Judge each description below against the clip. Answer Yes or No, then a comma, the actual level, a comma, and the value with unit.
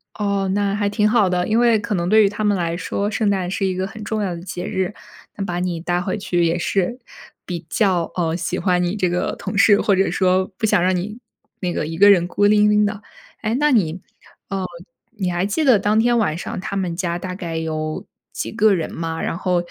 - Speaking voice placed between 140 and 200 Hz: Yes, high, 190 Hz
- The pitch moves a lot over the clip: No, average, 2.9 semitones